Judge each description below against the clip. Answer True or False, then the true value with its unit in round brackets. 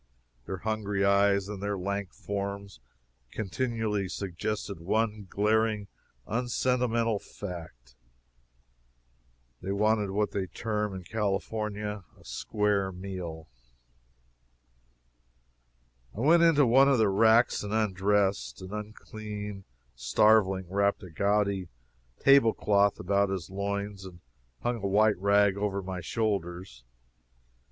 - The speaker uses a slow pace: True (110 wpm)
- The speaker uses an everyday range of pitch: False (2.0 semitones)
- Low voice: True (100 Hz)